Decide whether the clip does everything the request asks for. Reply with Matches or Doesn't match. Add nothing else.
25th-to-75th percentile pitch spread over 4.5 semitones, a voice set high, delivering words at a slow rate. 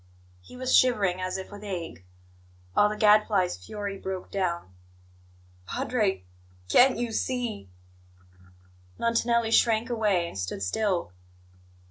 Matches